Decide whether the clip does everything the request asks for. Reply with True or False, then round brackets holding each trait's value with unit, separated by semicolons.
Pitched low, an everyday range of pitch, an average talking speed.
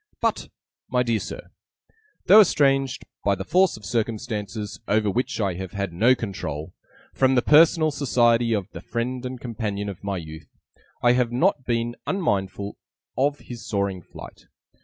True (115 Hz; 4.5 semitones; 160 wpm)